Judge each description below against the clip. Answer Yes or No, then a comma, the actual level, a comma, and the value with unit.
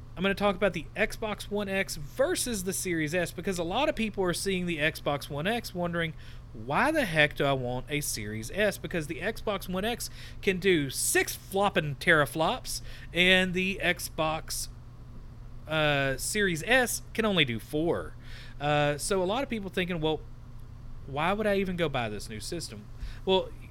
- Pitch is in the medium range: Yes, medium, 165 Hz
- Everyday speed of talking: Yes, average, 180 wpm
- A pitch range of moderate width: No, wide, 7.9 semitones